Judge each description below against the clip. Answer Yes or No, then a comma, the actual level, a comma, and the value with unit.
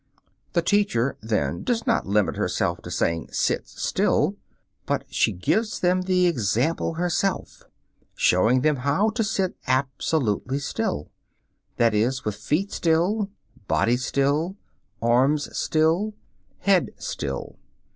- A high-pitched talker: No, medium, 150 Hz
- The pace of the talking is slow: Yes, slow, 120 wpm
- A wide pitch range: Yes, wide, 7.7 semitones